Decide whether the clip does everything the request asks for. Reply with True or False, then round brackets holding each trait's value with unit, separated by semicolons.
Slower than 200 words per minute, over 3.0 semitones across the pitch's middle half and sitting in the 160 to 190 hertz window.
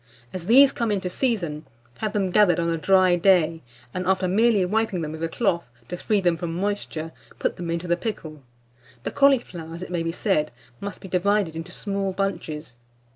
True (190 wpm; 3.5 semitones; 185 Hz)